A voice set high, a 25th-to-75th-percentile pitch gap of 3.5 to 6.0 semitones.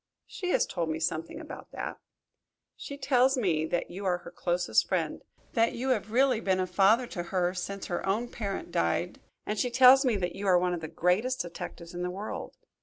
Yes: high, 195 Hz; wide, 5.5 semitones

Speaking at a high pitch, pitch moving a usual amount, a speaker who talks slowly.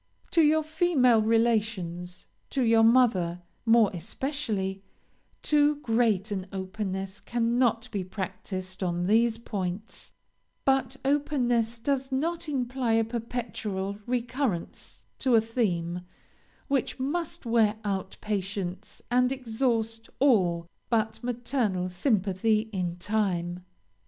Yes: high, 225 Hz; average, 4.8 semitones; slow, 105 wpm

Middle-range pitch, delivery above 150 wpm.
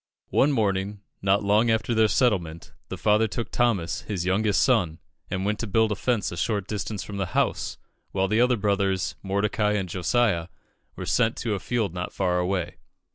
No: low, 100 Hz; average, 185 wpm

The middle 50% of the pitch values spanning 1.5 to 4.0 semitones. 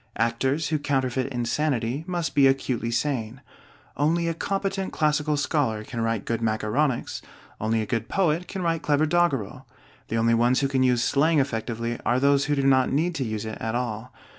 No: average, 4.6 semitones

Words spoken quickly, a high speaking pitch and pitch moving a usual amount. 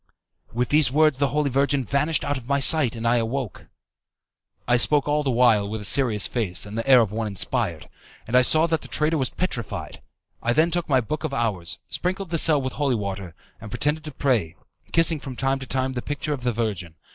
No: fast, 225 wpm; low, 130 Hz; average, 4.6 semitones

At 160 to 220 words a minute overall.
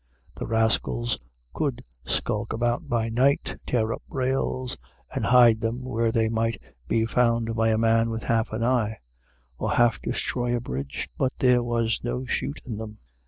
Yes: average, 165 wpm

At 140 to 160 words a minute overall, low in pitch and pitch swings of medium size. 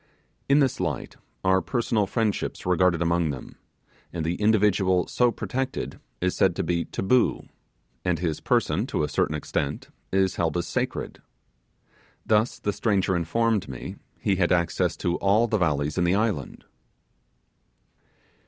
Yes: average, 145 wpm; very low, 95 Hz; average, 4.2 semitones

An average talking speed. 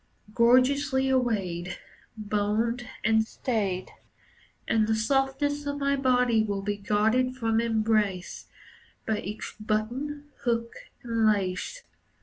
No: slow, 110 wpm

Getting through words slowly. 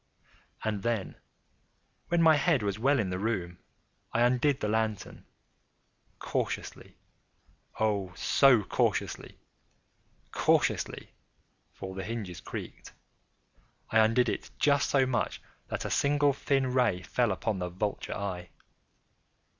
Yes: slow, 110 wpm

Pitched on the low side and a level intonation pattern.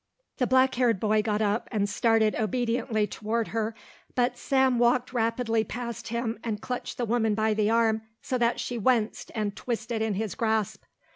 No: high, 225 Hz; narrow, 2.0 semitones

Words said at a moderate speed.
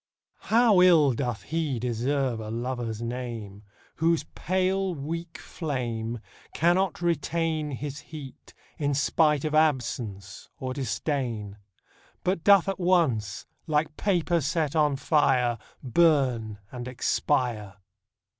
No: slow, 110 wpm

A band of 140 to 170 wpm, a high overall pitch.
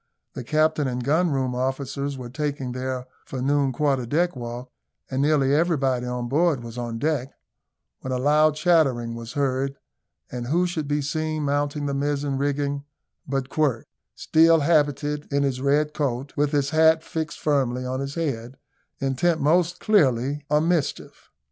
No: average, 160 wpm; medium, 140 Hz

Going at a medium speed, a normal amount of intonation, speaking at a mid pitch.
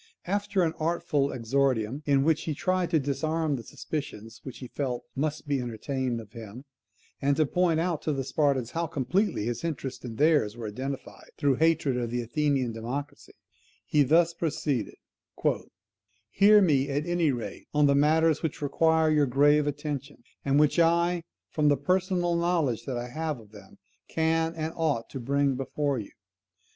Yes: average, 170 wpm; average, 3.8 semitones; medium, 145 Hz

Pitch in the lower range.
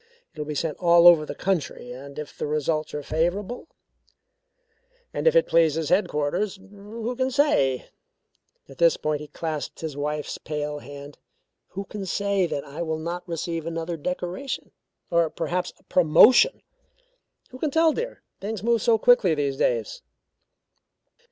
No: medium, 170 Hz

